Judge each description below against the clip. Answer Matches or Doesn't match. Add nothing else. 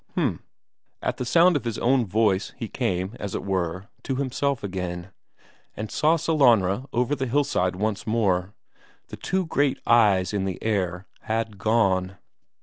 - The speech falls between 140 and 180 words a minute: Matches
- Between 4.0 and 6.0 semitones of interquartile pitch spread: Matches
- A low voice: Matches